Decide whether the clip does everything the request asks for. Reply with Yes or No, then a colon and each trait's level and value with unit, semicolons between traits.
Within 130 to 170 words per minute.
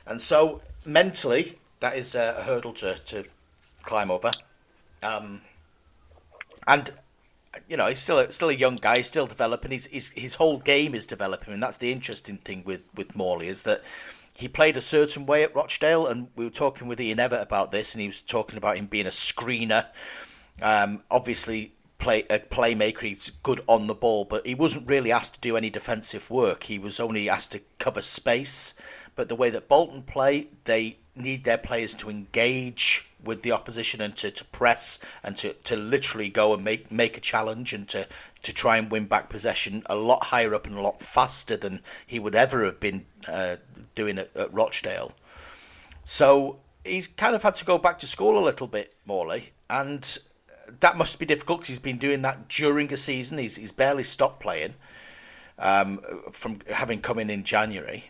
No: average, 195 wpm